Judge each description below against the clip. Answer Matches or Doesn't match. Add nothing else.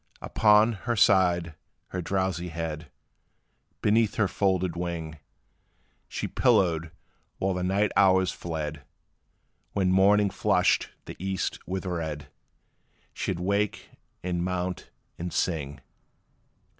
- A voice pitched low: Matches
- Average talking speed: Doesn't match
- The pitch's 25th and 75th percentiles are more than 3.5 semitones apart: Doesn't match